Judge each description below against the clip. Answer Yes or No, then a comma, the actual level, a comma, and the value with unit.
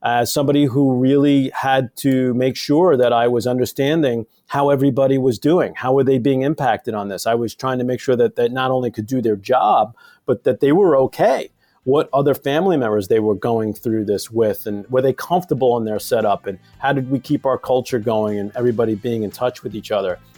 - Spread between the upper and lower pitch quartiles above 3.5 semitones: No, average, 2.9 semitones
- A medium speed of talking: No, fast, 220 wpm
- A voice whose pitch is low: Yes, low, 130 Hz